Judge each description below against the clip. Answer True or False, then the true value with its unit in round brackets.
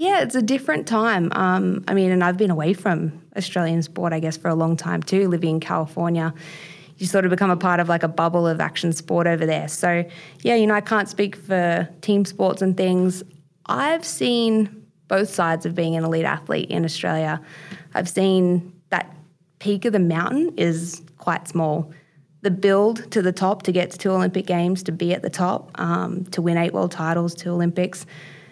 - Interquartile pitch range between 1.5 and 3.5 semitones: True (2.6 semitones)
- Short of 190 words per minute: False (205 wpm)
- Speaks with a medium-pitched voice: True (175 Hz)